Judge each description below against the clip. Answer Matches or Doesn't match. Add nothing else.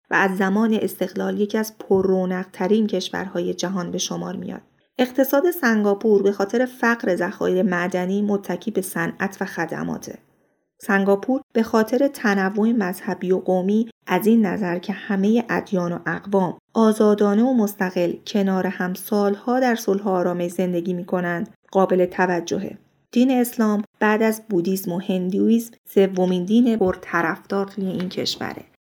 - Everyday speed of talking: Matches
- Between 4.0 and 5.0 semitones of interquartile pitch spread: Doesn't match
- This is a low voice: Doesn't match